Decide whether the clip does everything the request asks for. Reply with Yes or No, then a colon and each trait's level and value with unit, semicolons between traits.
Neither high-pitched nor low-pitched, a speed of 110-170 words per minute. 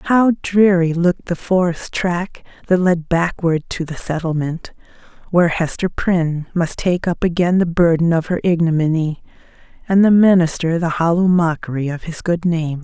Yes: medium, 170 Hz; average, 160 wpm